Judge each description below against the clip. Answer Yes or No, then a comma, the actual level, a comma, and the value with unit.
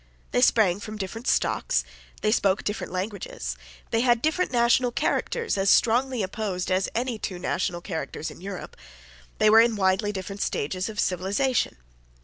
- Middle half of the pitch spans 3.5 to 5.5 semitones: Yes, average, 4.0 semitones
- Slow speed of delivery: No, average, 155 wpm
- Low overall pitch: No, high, 210 Hz